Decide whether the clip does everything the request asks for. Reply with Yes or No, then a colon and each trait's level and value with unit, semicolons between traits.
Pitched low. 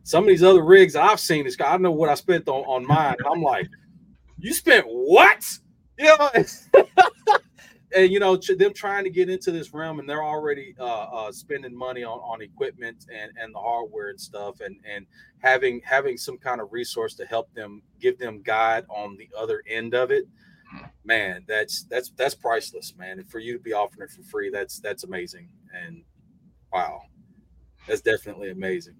No: medium, 185 Hz